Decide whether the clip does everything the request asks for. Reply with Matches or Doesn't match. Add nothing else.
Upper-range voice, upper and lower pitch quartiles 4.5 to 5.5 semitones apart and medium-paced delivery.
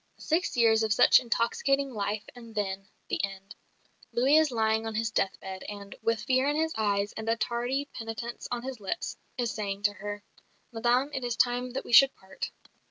Doesn't match